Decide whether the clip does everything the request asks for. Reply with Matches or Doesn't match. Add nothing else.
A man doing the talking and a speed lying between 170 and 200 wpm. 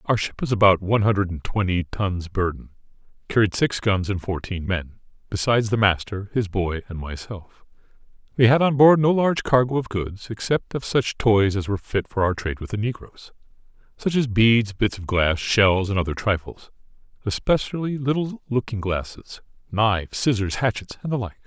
Matches